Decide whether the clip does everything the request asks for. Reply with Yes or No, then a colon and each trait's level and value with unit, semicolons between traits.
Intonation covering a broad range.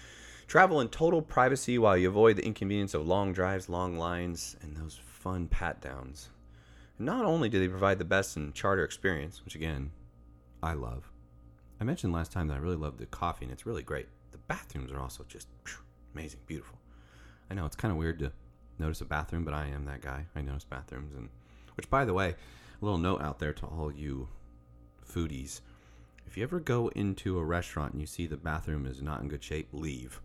Yes: wide, 6.8 semitones